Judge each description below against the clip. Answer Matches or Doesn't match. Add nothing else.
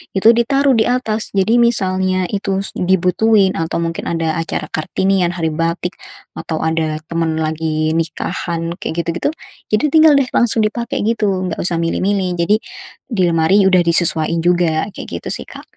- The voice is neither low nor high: Matches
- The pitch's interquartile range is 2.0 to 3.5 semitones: Doesn't match